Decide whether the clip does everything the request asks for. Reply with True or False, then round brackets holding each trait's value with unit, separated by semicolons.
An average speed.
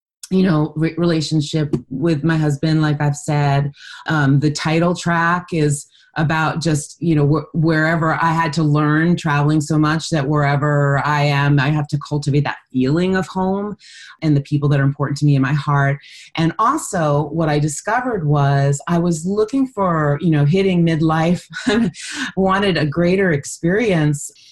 True (170 wpm)